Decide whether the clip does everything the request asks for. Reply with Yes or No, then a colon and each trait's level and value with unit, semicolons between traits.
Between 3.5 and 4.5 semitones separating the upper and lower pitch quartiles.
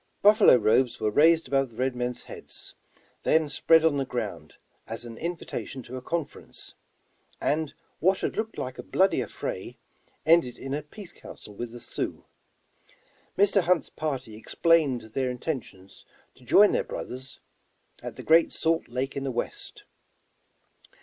No: average, 5.0 semitones